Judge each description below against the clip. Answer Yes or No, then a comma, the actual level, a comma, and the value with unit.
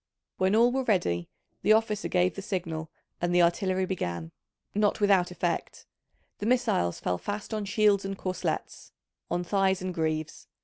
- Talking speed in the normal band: Yes, average, 160 wpm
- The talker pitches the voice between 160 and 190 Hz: Yes, medium, 185 Hz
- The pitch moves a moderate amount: Yes, average, 3.2 semitones